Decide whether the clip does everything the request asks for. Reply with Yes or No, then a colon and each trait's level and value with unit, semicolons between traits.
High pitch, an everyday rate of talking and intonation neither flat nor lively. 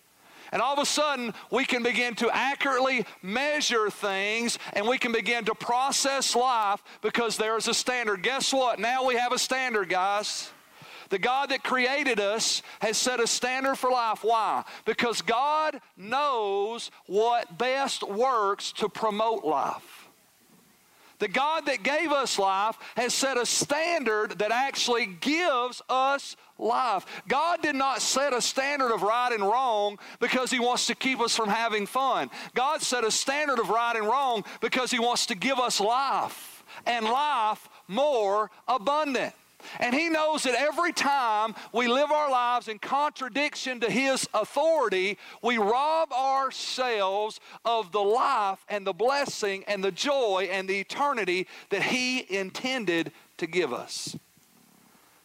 Yes: high, 245 Hz; average, 155 wpm; average, 4.0 semitones